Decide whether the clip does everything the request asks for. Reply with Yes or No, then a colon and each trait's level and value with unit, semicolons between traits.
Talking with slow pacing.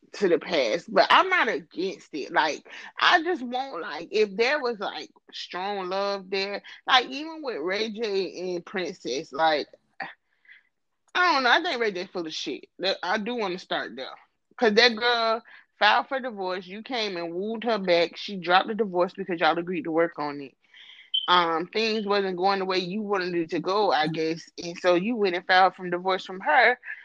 No: average, 200 wpm